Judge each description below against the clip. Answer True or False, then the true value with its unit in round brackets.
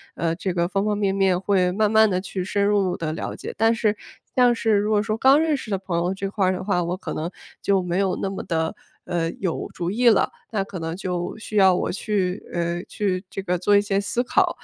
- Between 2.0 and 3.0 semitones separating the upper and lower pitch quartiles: True (2.6 semitones)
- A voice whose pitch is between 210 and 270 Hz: False (195 Hz)